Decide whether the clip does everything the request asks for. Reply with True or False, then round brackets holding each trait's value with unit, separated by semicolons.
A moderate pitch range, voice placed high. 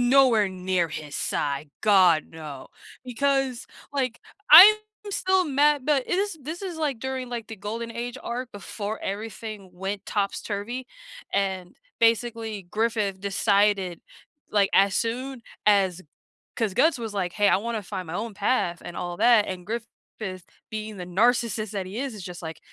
True (4.2 semitones; 215 Hz)